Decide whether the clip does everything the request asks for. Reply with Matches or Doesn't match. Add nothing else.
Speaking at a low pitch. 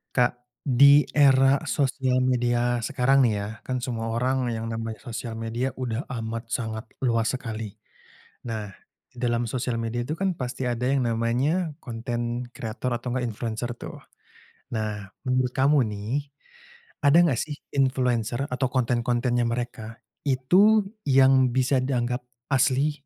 Matches